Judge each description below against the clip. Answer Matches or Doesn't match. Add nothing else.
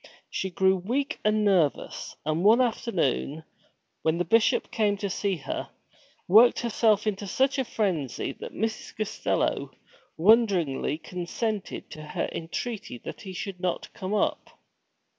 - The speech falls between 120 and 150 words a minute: Matches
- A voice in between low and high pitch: Doesn't match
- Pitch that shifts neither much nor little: Matches